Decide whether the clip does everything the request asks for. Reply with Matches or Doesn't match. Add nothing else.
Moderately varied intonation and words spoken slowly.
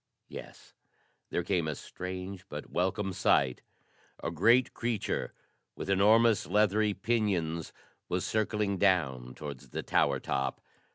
Matches